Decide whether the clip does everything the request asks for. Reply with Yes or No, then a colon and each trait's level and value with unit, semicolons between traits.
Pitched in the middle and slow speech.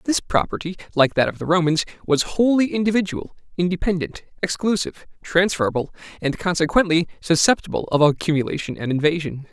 Yes: medium, 170 Hz; slow, 125 wpm